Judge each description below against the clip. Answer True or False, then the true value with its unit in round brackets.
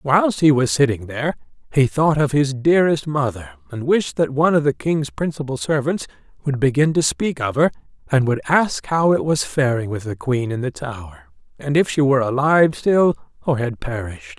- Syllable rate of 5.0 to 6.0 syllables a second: True (5.3 syllables/s)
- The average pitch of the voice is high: False (140 Hz)